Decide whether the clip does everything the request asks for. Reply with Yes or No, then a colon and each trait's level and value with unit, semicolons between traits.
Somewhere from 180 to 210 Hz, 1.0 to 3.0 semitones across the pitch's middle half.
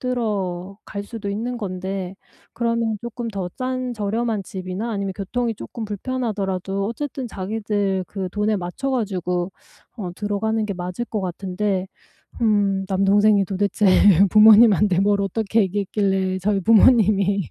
Yes: high, 205 Hz; narrow, 2.6 semitones